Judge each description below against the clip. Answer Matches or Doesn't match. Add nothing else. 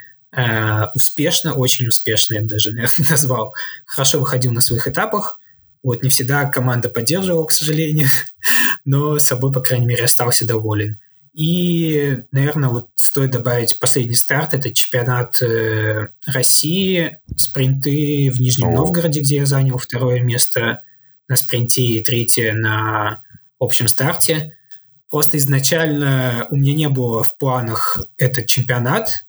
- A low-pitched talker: Matches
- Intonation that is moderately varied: Matches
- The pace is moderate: Matches